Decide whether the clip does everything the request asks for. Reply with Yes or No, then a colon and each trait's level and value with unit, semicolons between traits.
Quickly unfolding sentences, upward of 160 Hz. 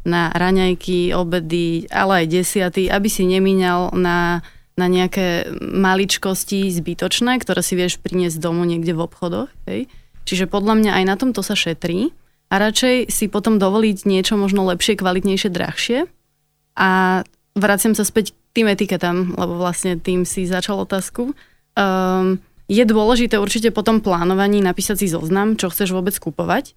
No: average, 150 wpm; high, 190 Hz